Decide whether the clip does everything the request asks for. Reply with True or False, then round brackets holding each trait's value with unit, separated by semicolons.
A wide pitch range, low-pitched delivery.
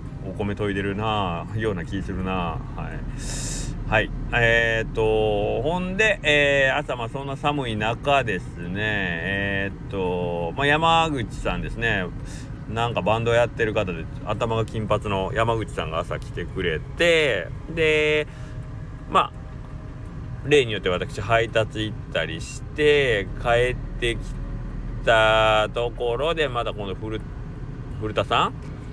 False (4.4 semitones; 115 Hz)